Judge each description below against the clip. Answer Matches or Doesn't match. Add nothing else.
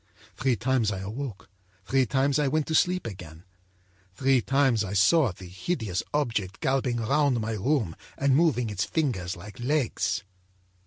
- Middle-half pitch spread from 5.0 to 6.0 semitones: Matches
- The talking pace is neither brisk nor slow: Matches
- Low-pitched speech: Matches